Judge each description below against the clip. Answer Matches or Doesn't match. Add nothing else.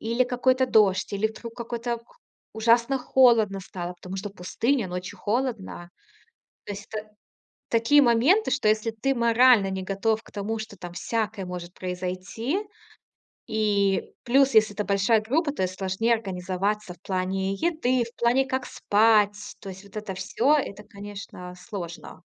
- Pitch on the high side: Matches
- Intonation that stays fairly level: Doesn't match